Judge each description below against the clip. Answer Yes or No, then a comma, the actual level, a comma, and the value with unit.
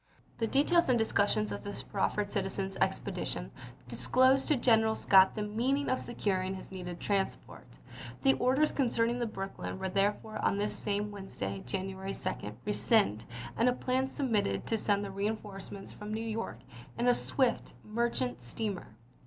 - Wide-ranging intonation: No, average, 3.5 semitones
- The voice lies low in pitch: No, high, 210 Hz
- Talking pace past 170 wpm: No, average, 160 wpm